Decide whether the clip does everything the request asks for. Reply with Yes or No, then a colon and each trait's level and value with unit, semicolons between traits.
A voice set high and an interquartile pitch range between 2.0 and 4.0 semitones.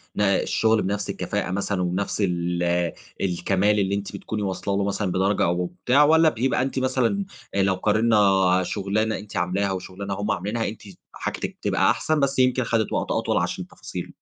No: low, 100 Hz; average, 3.1 semitones